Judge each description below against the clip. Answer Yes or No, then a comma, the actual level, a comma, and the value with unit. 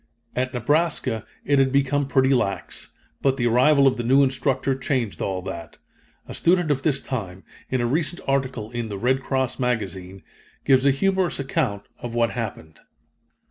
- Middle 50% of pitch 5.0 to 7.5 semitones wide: No, average, 3.2 semitones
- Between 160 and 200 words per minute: Yes, average, 170 wpm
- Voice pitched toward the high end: No, low, 130 Hz